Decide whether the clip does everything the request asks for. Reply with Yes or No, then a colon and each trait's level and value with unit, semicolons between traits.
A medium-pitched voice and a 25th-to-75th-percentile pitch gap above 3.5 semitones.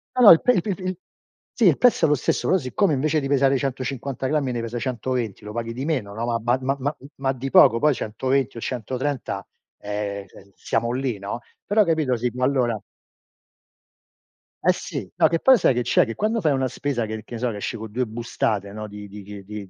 No: low, 125 Hz; average, 4.0 semitones